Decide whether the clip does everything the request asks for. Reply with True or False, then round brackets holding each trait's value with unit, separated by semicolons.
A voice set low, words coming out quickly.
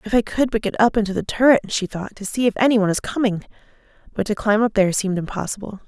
False (215 Hz; 255 wpm)